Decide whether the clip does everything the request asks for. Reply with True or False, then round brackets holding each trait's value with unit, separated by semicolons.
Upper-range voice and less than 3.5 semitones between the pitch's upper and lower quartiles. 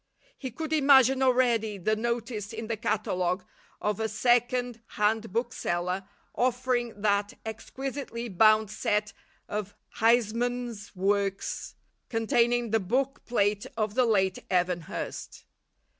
True (225 Hz; 3.0 semitones)